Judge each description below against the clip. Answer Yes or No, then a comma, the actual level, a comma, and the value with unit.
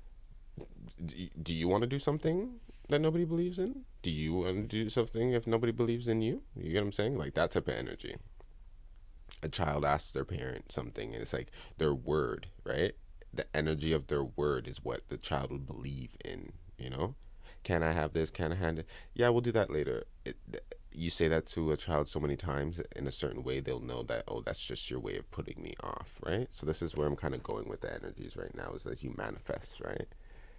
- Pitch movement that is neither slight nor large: No, wide, 7.5 semitones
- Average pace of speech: No, fast, 230 wpm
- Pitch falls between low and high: No, very low, 85 Hz